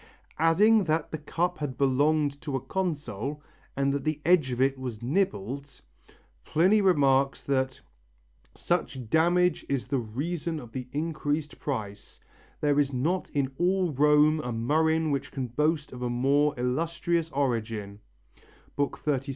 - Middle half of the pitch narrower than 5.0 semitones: Yes, average, 3.6 semitones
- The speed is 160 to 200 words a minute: No, average, 145 wpm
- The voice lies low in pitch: No, medium, 145 Hz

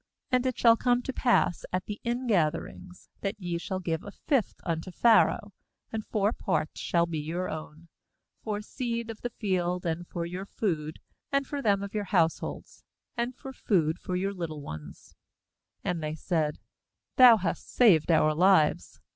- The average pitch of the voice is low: No, medium, 185 Hz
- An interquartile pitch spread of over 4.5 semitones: Yes, wide, 5.5 semitones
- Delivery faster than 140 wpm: Yes, average, 170 wpm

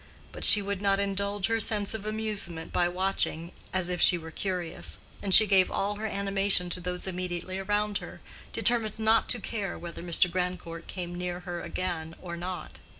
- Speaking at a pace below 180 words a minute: No, average, 185 wpm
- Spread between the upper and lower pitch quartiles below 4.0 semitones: Yes, narrow, 2.5 semitones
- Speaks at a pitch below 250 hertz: Yes, medium, 185 Hz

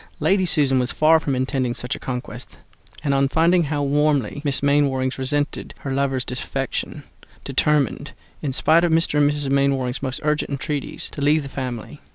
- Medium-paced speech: Yes, average, 175 wpm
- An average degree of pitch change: No, narrow, 2.2 semitones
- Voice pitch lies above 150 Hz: No, medium, 140 Hz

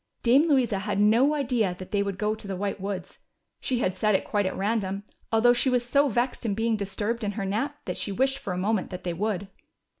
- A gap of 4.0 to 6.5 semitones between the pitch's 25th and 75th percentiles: No, average, 3.5 semitones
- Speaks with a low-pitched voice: No, high, 215 Hz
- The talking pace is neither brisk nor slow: No, fast, 240 wpm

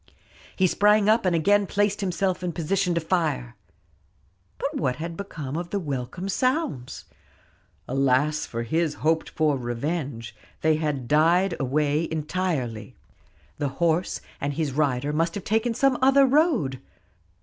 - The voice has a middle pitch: Yes, medium, 160 Hz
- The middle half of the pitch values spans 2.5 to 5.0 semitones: No, wide, 5.6 semitones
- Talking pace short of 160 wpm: Yes, average, 140 wpm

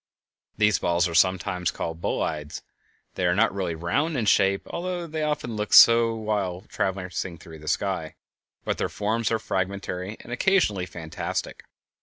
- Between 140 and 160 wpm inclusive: Yes, average, 150 wpm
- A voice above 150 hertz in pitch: No, very low, 95 Hz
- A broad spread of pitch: No, average, 4.3 semitones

